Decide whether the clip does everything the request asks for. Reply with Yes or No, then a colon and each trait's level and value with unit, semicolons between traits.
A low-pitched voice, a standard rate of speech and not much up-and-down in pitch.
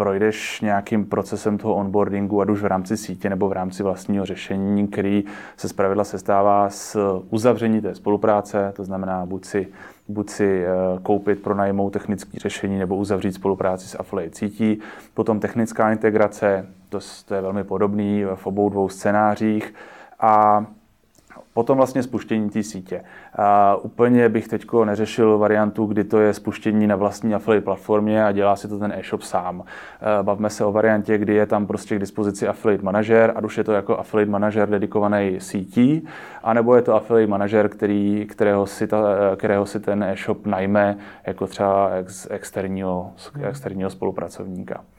Yes: low, 105 Hz; average, 155 wpm; narrow, 1.4 semitones